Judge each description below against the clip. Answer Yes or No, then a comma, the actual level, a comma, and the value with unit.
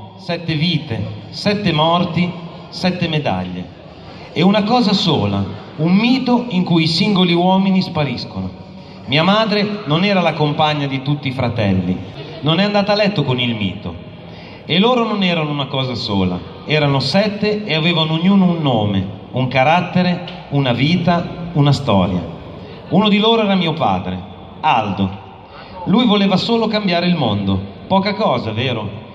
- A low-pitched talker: No, medium, 155 Hz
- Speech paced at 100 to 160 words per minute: Yes, average, 150 wpm